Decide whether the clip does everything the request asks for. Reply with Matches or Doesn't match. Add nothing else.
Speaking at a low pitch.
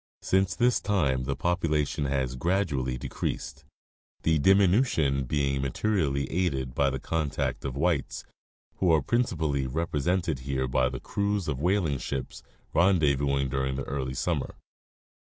Matches